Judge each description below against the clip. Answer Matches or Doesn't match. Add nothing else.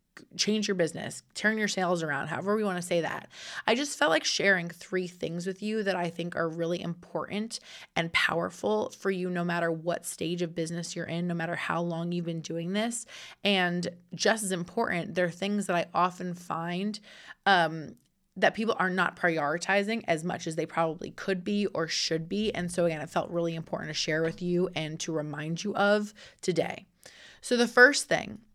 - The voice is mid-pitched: Matches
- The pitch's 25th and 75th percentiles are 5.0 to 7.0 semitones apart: Doesn't match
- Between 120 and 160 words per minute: Doesn't match